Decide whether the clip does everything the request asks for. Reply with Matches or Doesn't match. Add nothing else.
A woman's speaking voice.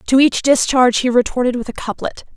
Matches